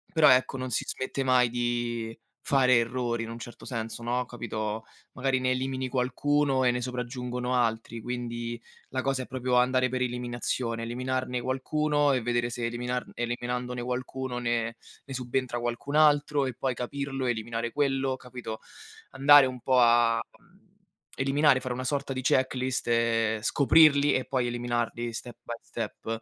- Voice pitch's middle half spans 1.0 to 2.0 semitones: Yes, narrow, 1.7 semitones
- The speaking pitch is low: Yes, low, 125 Hz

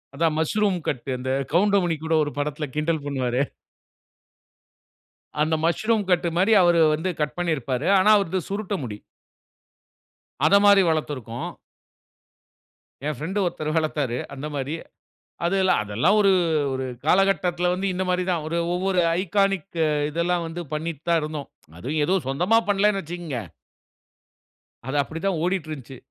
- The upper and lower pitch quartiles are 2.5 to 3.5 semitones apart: No, average, 4.1 semitones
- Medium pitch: Yes, medium, 165 Hz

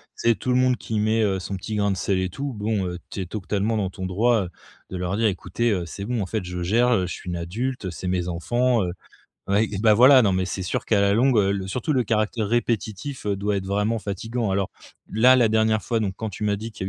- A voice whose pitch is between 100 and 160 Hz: Yes, low, 105 Hz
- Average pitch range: Yes, average, 3.3 semitones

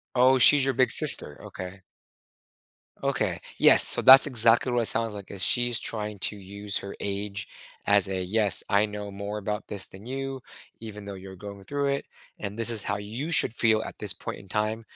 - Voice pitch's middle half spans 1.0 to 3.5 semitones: Yes, average, 3.0 semitones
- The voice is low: Yes, low, 105 Hz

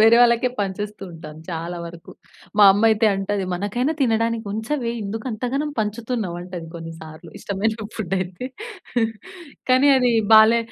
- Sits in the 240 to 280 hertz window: No, high, 210 Hz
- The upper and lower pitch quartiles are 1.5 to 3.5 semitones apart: No, average, 4.2 semitones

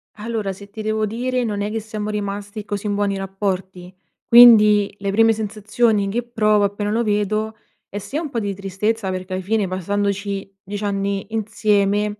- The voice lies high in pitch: Yes, high, 205 Hz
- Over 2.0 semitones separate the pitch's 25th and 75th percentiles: No, narrow, 1.6 semitones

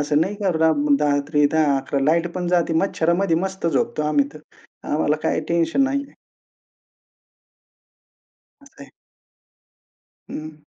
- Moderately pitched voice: Yes, medium, 160 Hz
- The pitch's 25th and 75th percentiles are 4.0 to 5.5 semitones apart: No, average, 2.9 semitones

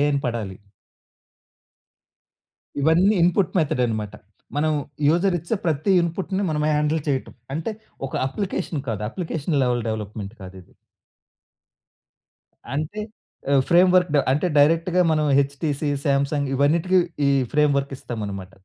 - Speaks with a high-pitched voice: No, medium, 150 Hz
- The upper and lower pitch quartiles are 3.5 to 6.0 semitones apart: Yes, average, 4.7 semitones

